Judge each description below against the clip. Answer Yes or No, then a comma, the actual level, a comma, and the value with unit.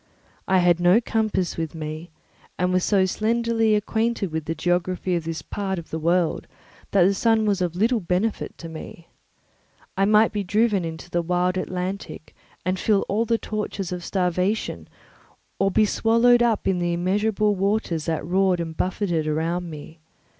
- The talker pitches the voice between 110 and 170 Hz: No, medium, 185 Hz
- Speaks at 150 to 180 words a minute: Yes, average, 170 wpm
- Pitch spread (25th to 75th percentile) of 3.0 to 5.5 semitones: Yes, average, 3.7 semitones